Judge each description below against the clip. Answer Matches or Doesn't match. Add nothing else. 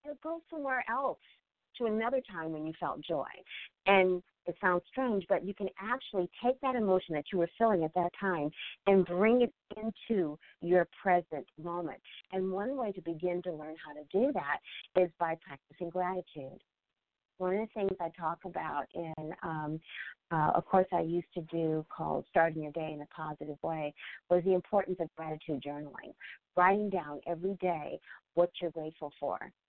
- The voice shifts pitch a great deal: Doesn't match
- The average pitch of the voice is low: Doesn't match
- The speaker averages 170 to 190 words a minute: Matches